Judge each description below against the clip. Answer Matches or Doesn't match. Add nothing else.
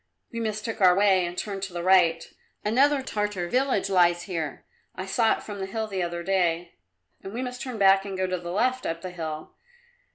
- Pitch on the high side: Matches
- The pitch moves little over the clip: Doesn't match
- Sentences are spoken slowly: Doesn't match